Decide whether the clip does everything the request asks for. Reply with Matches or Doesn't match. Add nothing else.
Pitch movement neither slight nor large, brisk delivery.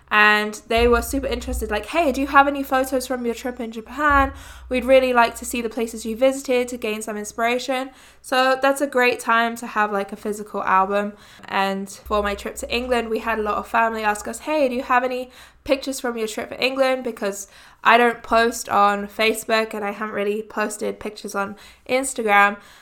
Matches